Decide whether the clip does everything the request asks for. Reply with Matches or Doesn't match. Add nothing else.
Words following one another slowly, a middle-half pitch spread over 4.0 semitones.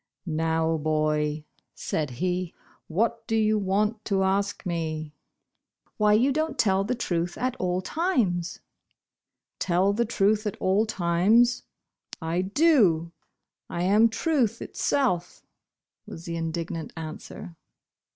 Matches